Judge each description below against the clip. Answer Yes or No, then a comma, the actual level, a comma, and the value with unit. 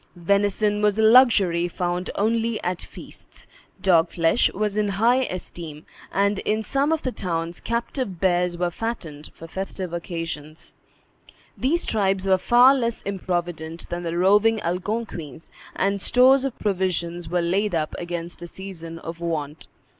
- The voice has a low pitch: No, medium, 185 Hz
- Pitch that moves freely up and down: No, average, 4.0 semitones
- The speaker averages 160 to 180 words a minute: No, average, 145 wpm